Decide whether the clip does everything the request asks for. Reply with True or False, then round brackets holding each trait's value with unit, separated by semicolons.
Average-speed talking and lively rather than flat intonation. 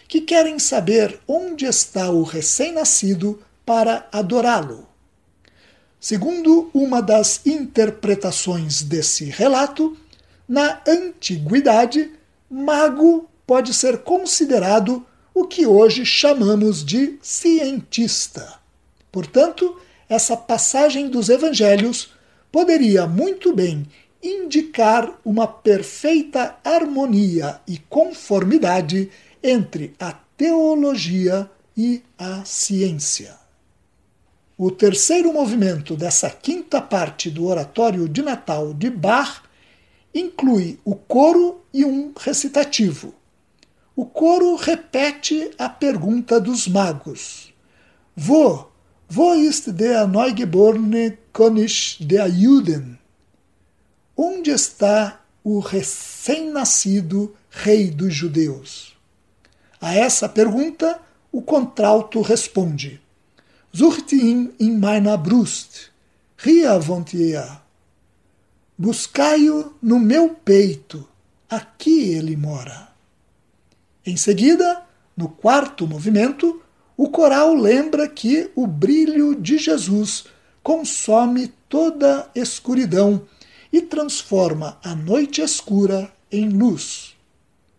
False (90 wpm; 7.8 semitones)